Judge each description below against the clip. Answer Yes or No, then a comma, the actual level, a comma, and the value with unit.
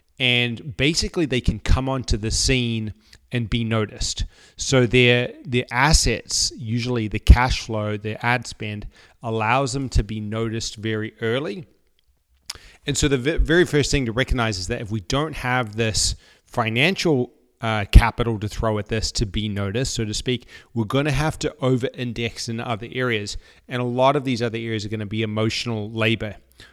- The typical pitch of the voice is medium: No, low, 115 Hz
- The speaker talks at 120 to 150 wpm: No, average, 180 wpm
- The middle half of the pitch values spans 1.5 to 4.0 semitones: Yes, average, 2.8 semitones